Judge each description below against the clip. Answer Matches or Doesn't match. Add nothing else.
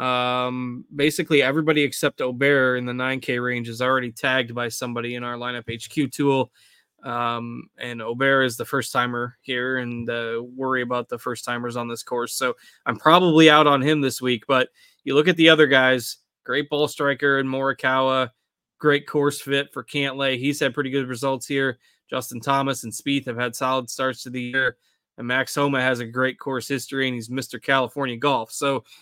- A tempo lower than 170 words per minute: Doesn't match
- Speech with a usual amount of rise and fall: Doesn't match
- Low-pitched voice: Matches